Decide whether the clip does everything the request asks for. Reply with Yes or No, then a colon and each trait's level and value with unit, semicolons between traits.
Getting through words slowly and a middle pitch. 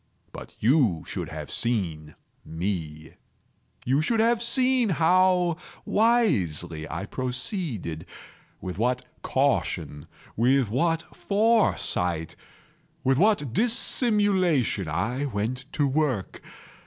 No: slow, 85 wpm; low, 130 Hz